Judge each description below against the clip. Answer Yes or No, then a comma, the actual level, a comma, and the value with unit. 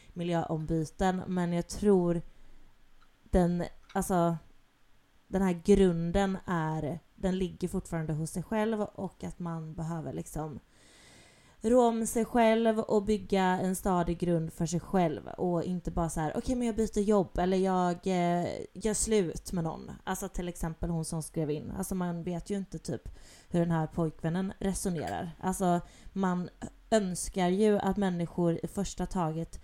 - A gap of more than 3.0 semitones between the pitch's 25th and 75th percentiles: No, average, 2.7 semitones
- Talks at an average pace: Yes, average, 160 wpm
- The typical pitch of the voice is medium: Yes, medium, 180 Hz